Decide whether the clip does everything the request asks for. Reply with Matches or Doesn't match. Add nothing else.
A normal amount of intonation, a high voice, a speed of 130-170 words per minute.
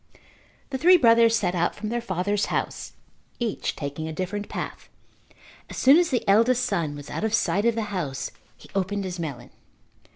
Doesn't match